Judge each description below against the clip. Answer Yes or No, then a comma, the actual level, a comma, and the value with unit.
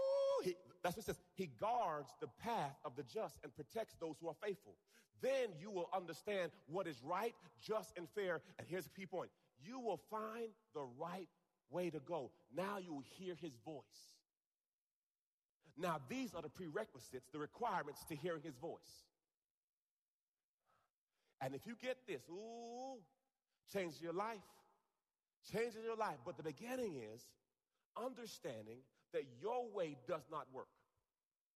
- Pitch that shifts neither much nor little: No, wide, 6.1 semitones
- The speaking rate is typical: Yes, average, 150 wpm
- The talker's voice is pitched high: No, medium, 180 Hz